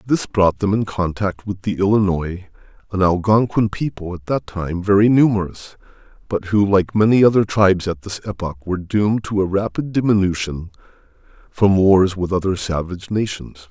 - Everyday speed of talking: Yes, average, 160 wpm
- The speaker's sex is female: No, male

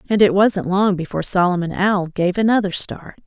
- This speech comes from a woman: Yes, female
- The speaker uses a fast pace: No, average, 185 wpm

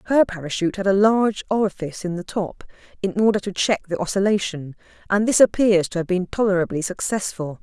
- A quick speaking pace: No, average, 180 wpm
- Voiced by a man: No, female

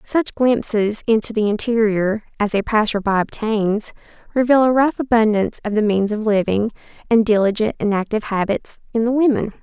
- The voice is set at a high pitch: Yes, high, 220 Hz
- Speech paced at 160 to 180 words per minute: Yes, average, 170 wpm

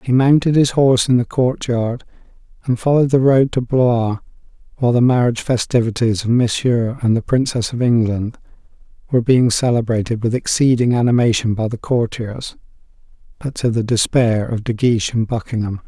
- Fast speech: No, average, 160 wpm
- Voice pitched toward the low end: Yes, low, 120 Hz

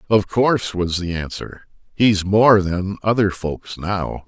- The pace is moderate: Yes, average, 155 wpm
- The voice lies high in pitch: No, very low, 95 Hz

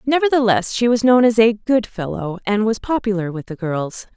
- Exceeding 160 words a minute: Yes, average, 200 wpm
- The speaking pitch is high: Yes, high, 220 Hz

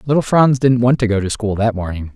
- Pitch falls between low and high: No, low, 115 Hz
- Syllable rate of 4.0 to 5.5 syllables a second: No, 6.0 syllables/s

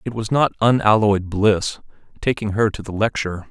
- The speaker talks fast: No, average, 170 wpm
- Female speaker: No, male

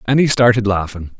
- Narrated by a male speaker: Yes, male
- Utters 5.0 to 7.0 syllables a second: Yes, 5.7 syllables/s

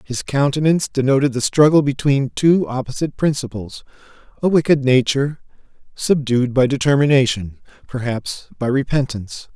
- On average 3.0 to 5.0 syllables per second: No, 5.3 syllables/s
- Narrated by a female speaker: No, male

